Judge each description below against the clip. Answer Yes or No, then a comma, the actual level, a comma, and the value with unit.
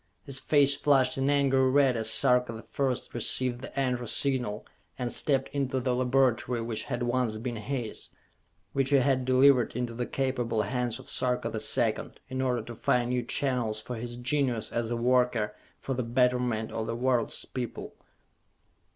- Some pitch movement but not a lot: No, narrow, 2.0 semitones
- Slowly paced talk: No, average, 175 wpm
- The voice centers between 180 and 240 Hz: No, low, 125 Hz